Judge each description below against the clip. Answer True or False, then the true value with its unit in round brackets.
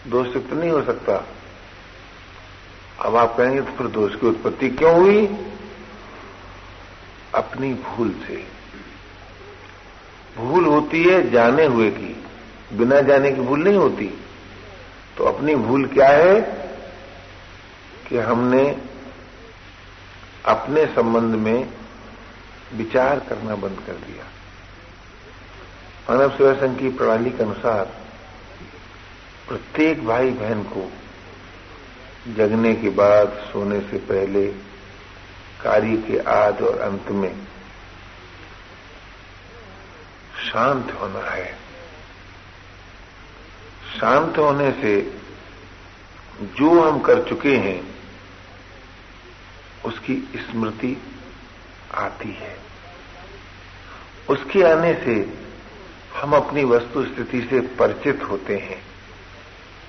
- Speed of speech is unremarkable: False (95 wpm)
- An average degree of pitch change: True (4.3 semitones)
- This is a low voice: True (100 Hz)